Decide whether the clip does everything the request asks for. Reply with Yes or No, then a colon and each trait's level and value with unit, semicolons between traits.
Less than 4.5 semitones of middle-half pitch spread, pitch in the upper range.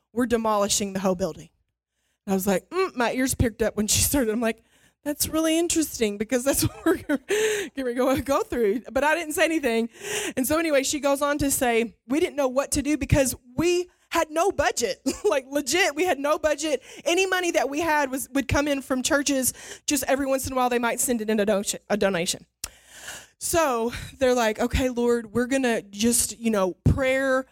No: average, 4.8 semitones; very high, 270 Hz